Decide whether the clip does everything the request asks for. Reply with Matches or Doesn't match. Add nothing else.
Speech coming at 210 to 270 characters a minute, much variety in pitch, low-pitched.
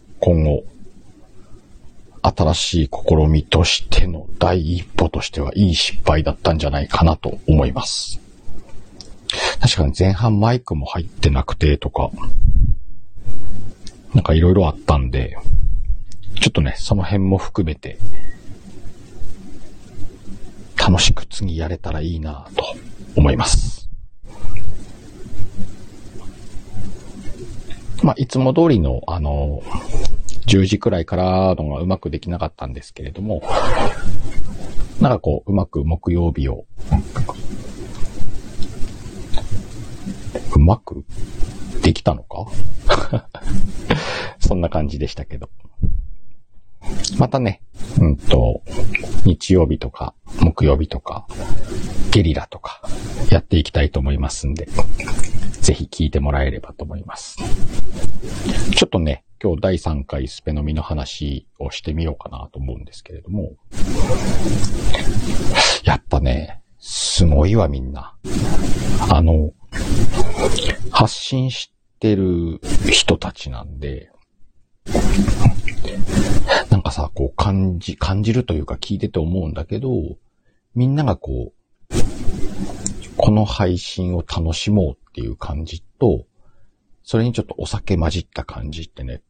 Doesn't match